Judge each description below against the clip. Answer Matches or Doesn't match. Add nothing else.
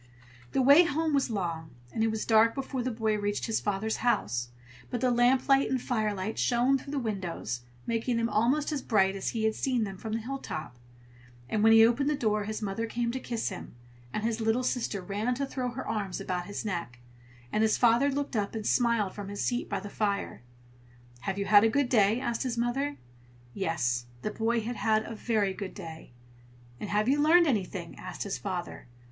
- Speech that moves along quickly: Matches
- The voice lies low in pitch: Doesn't match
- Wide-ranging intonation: Doesn't match